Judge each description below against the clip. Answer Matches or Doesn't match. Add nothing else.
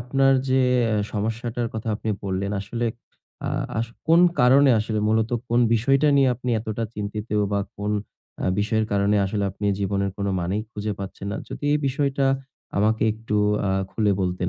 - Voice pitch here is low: Matches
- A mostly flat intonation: Doesn't match